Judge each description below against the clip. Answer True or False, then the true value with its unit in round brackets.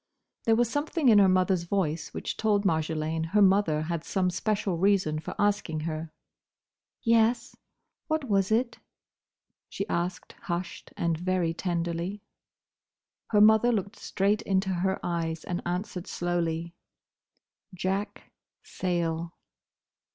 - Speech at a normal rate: False (120 wpm)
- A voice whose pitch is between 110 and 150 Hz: False (185 Hz)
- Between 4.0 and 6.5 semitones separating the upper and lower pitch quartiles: False (3.5 semitones)